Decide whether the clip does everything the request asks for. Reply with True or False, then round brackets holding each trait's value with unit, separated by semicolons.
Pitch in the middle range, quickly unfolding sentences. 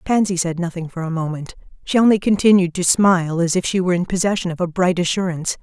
True (180 Hz; 225 wpm)